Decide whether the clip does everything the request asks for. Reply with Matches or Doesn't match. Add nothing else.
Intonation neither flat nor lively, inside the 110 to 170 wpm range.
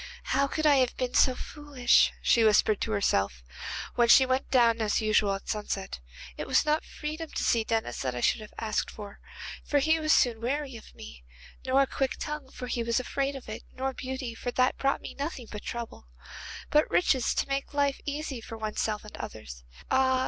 Doesn't match